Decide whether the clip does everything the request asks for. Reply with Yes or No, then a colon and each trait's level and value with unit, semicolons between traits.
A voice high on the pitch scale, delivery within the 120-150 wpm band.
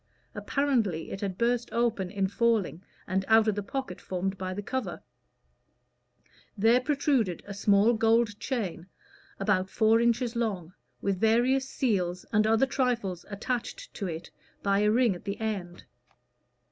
Yes: high, 215 Hz; average, 145 wpm